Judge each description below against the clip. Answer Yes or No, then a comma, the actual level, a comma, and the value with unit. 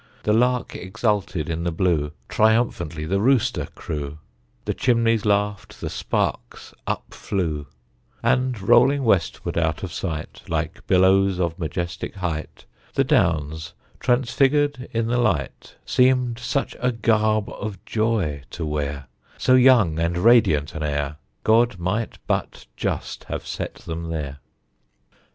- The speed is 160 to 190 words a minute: No, slow, 135 wpm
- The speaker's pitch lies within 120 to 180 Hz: No, very low, 95 Hz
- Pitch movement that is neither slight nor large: No, wide, 6.5 semitones